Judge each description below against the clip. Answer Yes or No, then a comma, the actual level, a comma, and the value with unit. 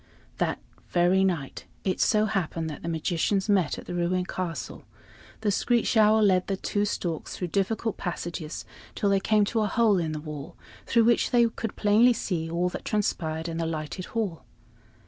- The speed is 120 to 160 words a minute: No, average, 185 wpm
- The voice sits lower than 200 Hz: Yes, medium, 185 Hz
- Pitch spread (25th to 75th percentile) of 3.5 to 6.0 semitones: Yes, average, 4.3 semitones